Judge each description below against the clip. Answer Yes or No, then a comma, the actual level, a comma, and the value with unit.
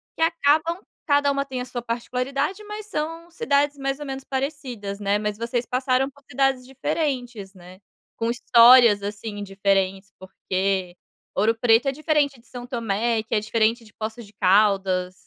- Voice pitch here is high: Yes, high, 240 Hz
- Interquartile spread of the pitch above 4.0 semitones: Yes, average, 5.2 semitones